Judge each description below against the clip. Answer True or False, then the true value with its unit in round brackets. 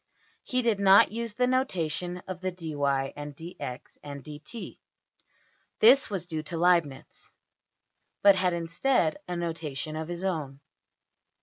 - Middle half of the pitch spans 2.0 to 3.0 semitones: False (3.9 semitones)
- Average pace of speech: False (125 wpm)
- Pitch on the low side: False (170 Hz)